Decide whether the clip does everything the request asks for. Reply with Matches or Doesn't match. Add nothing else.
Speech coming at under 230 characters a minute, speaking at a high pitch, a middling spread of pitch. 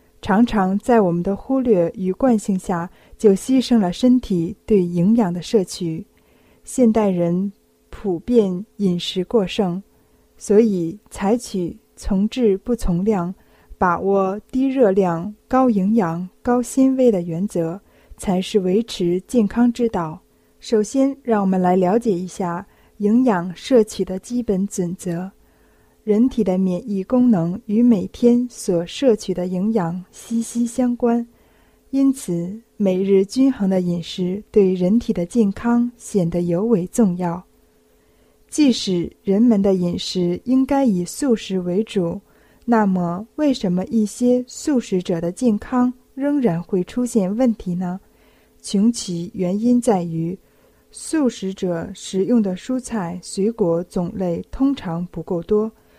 Matches